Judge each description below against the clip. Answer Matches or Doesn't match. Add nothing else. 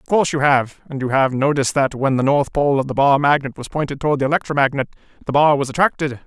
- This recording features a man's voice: Matches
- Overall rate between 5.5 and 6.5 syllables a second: Doesn't match